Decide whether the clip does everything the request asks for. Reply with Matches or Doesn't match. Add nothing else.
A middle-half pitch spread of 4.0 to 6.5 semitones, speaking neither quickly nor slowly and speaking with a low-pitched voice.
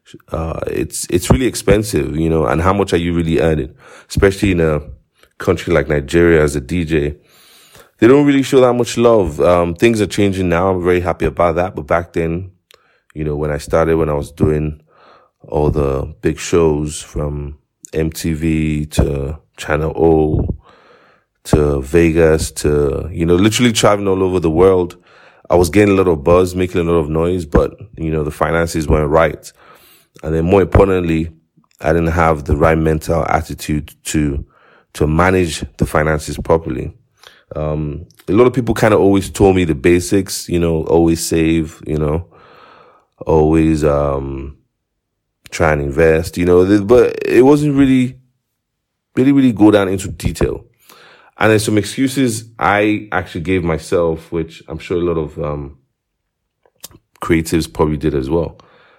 Doesn't match